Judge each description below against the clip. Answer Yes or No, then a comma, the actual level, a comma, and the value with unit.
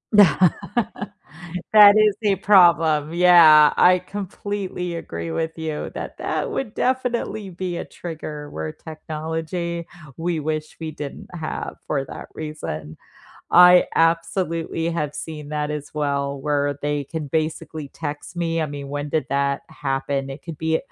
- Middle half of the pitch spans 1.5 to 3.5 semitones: Yes, average, 3.0 semitones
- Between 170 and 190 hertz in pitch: No, medium, 160 Hz